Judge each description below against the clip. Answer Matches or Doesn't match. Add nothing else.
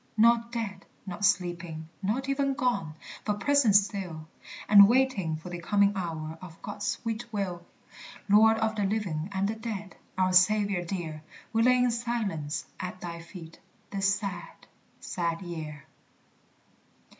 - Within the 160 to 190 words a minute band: Doesn't match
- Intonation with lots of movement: Doesn't match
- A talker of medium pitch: Doesn't match